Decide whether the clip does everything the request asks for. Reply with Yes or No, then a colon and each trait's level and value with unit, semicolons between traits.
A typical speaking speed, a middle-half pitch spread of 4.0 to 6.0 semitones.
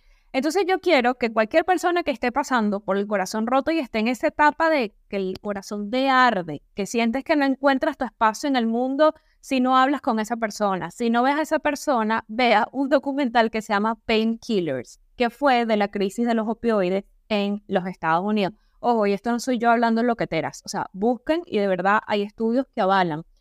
No: fast, 215 wpm; average, 4.7 semitones